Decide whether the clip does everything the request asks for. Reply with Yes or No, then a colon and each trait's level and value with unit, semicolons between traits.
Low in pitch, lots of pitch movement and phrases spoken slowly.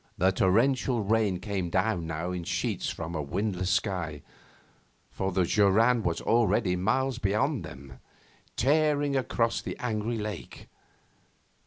No: low, 105 Hz; average, 4.7 semitones; slow, 130 wpm